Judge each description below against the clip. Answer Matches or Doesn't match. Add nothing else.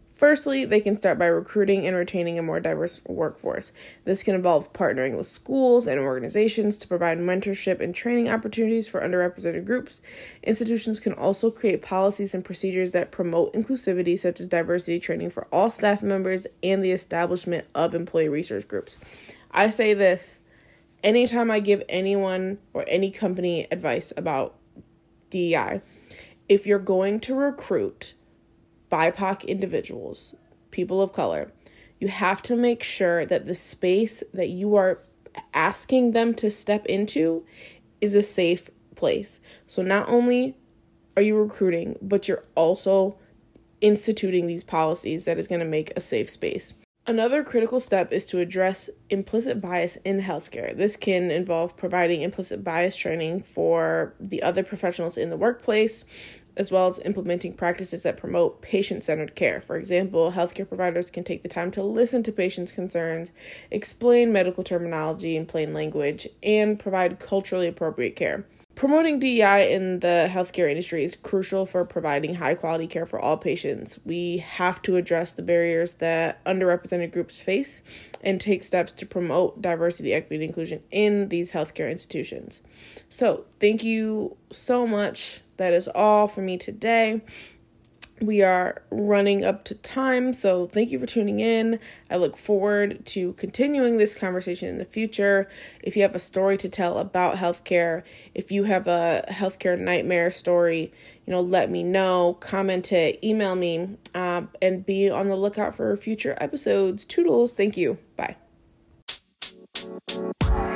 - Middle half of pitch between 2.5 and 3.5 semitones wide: Matches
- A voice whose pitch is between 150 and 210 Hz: Matches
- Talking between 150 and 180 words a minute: Matches